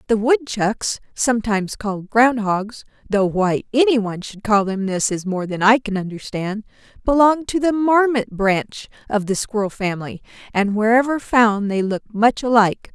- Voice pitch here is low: No, high, 220 Hz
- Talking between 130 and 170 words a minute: Yes, average, 165 wpm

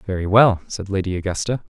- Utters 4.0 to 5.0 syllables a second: No, 5.9 syllables/s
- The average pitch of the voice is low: Yes, low, 100 Hz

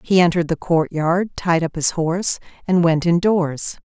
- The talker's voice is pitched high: No, medium, 170 Hz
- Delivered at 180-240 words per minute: No, average, 170 wpm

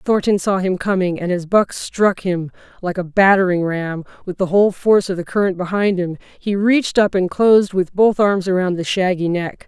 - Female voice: Yes, female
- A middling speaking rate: No, fast, 210 wpm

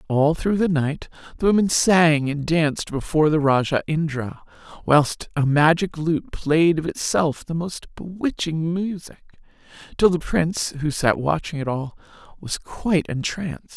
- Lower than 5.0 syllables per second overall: Yes, 4.5 syllables/s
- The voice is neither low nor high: Yes, medium, 160 Hz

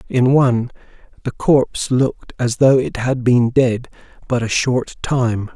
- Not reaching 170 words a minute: Yes, average, 160 wpm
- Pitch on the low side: Yes, low, 125 Hz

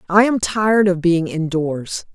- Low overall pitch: No, medium, 185 Hz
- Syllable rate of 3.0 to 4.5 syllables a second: Yes, 4.2 syllables/s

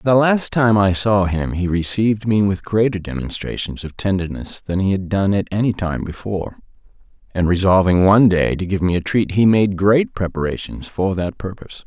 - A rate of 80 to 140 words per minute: No, average, 190 wpm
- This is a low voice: Yes, very low, 95 Hz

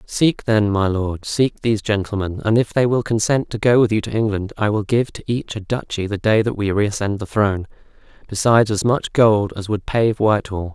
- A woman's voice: No, male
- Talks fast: Yes, fast, 225 wpm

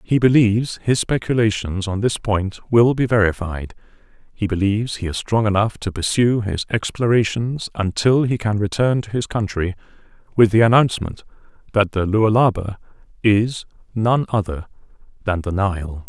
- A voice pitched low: Yes, low, 105 Hz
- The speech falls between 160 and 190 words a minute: No, average, 145 wpm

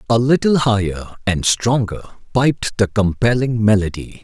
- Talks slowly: Yes, slow, 130 wpm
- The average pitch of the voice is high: No, low, 110 Hz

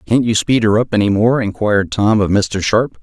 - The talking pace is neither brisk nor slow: No, fast, 240 wpm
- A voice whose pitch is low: Yes, low, 105 Hz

